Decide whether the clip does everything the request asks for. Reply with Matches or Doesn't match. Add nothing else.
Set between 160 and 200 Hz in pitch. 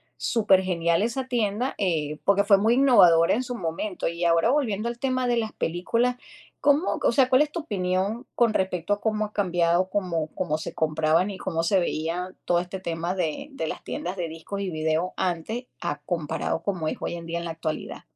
Matches